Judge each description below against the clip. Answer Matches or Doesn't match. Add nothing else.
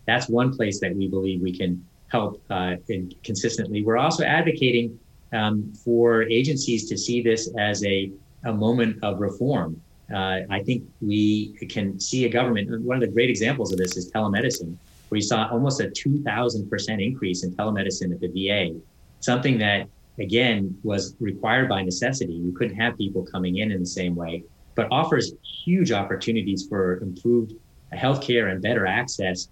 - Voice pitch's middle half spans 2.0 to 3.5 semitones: Doesn't match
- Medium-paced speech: Matches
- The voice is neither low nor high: Doesn't match